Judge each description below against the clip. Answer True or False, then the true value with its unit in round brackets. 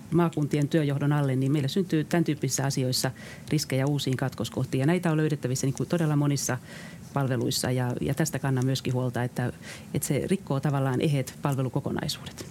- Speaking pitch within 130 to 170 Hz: True (140 Hz)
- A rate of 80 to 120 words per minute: False (145 wpm)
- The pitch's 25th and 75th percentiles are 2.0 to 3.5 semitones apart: True (2.9 semitones)